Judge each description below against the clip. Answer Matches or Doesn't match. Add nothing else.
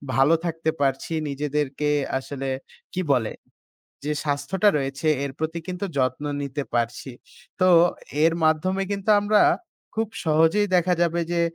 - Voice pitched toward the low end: Doesn't match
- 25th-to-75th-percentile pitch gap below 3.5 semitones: Doesn't match